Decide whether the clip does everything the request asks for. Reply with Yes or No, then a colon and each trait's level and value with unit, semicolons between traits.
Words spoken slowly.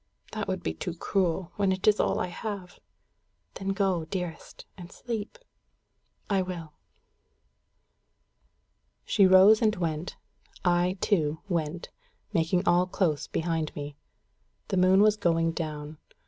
Yes: slow, 130 wpm